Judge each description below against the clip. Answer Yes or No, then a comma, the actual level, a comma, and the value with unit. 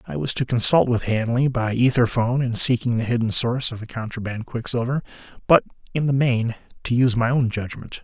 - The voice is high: No, low, 120 Hz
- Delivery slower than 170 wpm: No, average, 200 wpm